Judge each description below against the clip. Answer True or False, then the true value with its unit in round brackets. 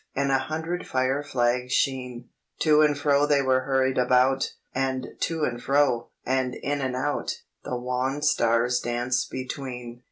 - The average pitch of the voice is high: False (130 Hz)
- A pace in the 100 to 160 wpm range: True (155 wpm)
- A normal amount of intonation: False (2.1 semitones)